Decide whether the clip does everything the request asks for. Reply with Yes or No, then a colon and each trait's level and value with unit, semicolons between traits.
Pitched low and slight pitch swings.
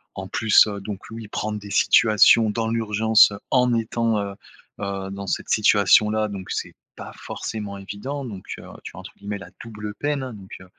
Yes: low, 105 Hz; narrow, 2.1 semitones